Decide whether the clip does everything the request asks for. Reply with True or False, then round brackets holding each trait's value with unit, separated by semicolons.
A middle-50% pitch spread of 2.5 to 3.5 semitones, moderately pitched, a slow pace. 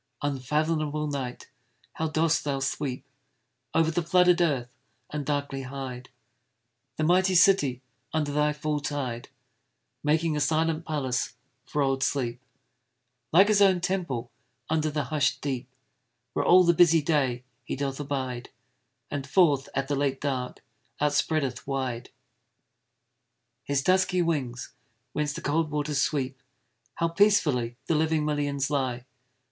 True (3.1 semitones; 145 Hz; 130 wpm)